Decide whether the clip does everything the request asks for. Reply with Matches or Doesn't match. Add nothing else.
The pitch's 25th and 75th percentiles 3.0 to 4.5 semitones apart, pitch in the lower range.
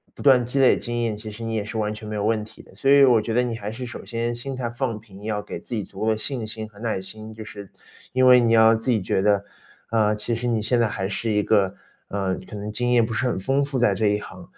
Doesn't match